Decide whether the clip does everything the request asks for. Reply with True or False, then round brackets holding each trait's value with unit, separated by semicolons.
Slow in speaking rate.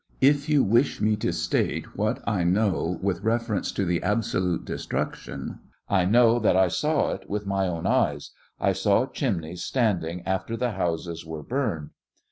False (170 wpm)